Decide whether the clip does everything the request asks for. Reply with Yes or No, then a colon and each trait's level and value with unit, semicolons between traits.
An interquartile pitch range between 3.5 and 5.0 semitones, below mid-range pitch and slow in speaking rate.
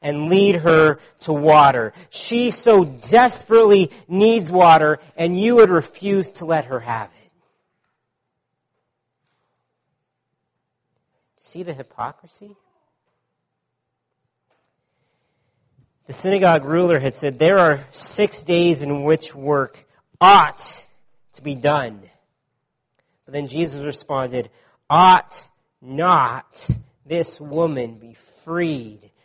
No: average, 4.6 semitones; medium, 155 Hz; slow, 100 wpm